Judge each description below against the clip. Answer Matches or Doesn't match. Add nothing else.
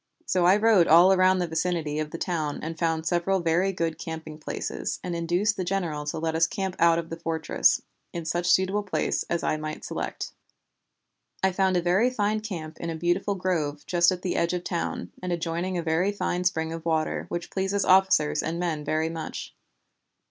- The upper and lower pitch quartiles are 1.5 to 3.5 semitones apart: Matches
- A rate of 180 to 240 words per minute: Matches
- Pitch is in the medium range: Matches